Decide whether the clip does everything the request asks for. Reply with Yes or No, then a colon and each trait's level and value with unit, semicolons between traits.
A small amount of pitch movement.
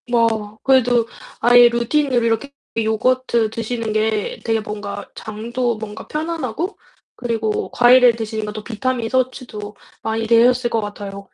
Yes: narrow, 2.3 semitones